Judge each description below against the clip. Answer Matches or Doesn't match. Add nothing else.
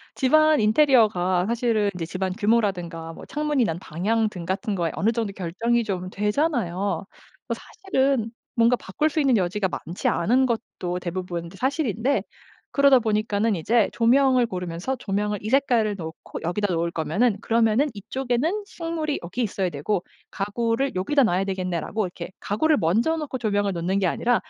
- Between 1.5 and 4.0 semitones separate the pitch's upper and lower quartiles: Doesn't match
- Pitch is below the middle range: Doesn't match